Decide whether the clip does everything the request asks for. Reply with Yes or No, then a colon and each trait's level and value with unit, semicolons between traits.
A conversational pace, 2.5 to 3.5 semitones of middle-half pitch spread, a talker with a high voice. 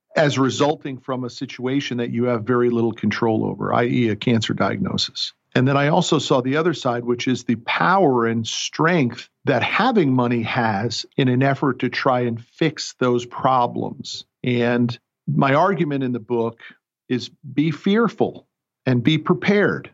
No: average, 165 wpm; average, 2.9 semitones; low, 125 Hz